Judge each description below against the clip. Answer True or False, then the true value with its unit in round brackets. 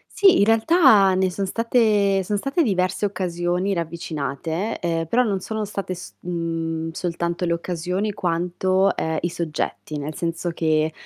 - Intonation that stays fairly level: False (3.3 semitones)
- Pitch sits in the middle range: True (180 Hz)